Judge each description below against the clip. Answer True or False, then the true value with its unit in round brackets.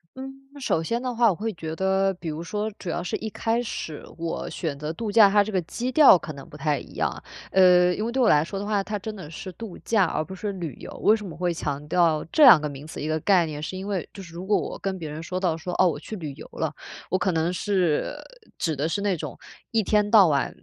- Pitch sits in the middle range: True (180 Hz)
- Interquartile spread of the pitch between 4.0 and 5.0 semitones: True (4.5 semitones)